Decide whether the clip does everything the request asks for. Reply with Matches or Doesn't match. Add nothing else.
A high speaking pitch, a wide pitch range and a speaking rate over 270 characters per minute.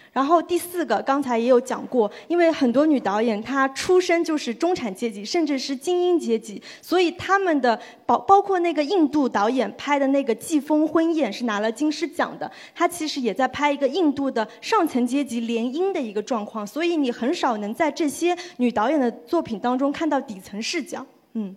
Matches